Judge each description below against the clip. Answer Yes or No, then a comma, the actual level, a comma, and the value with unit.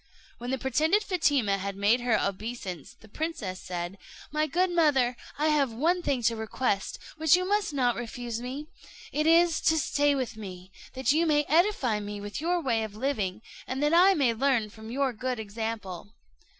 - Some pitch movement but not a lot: No, wide, 5.9 semitones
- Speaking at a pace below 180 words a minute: No, average, 185 wpm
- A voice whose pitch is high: Yes, very high, 255 Hz